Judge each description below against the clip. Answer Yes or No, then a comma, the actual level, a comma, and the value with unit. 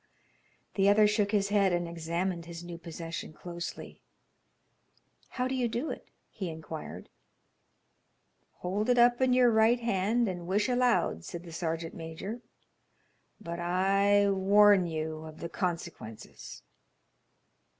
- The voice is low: No, high, 190 Hz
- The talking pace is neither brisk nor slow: No, slow, 130 wpm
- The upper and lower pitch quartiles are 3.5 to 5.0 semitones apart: Yes, average, 4.1 semitones